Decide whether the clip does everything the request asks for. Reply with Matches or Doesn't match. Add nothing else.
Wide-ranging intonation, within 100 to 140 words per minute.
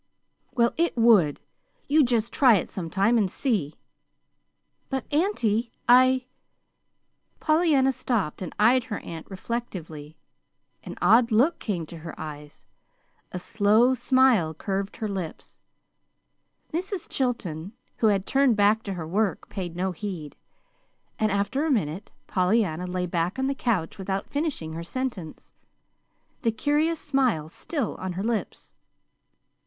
Matches